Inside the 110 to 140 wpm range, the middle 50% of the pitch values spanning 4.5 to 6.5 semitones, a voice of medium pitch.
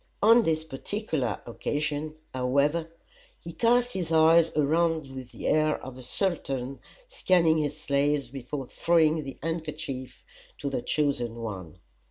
No: slow, 135 wpm; average, 3.6 semitones; medium, 150 Hz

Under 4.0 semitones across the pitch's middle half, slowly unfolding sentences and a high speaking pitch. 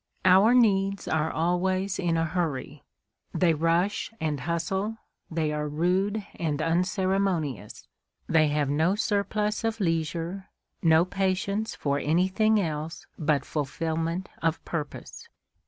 No: average, 3.6 semitones; slow, 120 wpm; medium, 170 Hz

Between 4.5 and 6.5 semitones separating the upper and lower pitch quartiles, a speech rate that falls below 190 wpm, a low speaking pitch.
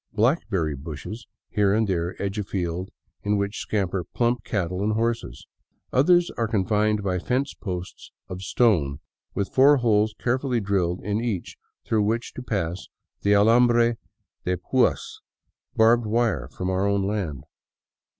No: average, 4.0 semitones; average, 150 wpm; low, 105 Hz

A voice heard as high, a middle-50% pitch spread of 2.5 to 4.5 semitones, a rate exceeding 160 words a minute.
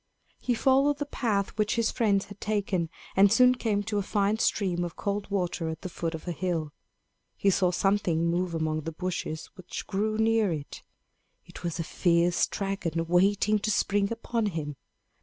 Yes: high, 195 Hz; average, 3.8 semitones; average, 180 wpm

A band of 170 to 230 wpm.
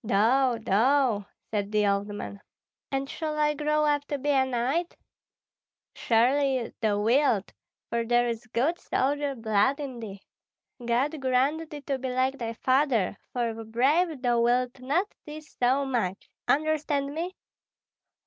No: average, 150 wpm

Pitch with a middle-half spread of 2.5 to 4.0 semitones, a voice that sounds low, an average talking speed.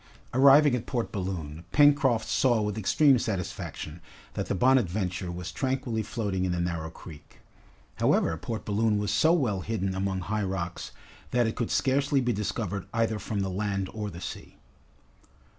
No: average, 4.6 semitones; low, 105 Hz; average, 160 wpm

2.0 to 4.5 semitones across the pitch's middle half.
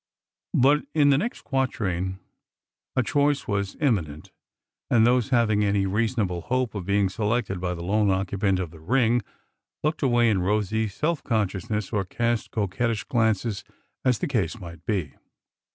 Yes: average, 4.2 semitones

